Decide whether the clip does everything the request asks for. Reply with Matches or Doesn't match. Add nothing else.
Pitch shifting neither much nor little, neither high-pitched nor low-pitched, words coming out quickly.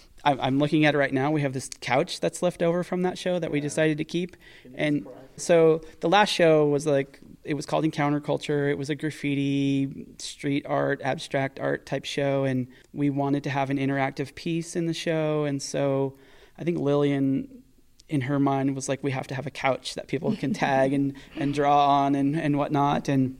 Doesn't match